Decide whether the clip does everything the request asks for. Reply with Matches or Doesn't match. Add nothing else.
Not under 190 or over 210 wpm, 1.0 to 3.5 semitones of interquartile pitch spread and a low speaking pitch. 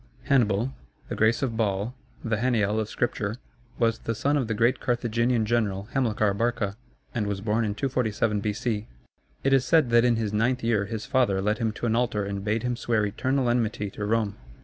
Matches